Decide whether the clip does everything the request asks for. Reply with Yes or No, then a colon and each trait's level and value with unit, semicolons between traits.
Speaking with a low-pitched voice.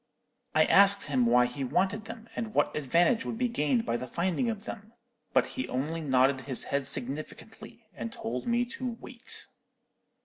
No: medium, 165 Hz